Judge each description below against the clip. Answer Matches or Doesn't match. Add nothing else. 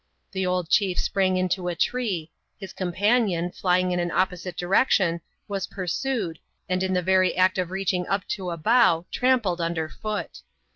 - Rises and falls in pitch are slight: Matches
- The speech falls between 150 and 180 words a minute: Matches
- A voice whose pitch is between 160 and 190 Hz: Matches